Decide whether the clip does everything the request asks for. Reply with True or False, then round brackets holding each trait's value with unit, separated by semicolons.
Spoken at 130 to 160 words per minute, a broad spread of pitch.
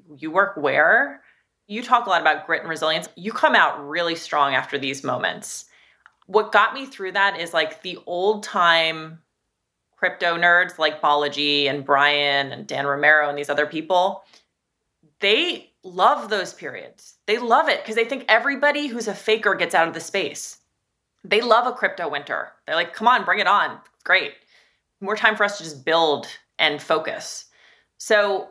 False (175 wpm; 5.8 semitones)